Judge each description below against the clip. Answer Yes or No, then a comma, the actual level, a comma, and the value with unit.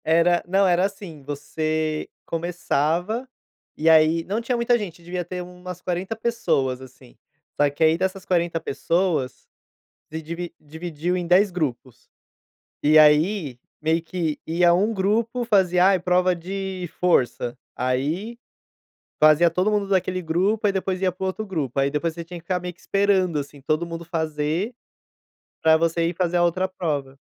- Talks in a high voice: No, medium, 175 Hz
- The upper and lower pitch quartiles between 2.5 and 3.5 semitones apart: Yes, average, 3.1 semitones